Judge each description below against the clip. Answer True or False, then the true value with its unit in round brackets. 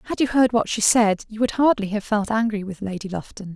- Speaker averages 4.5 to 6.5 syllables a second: True (5.8 syllables/s)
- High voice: True (215 Hz)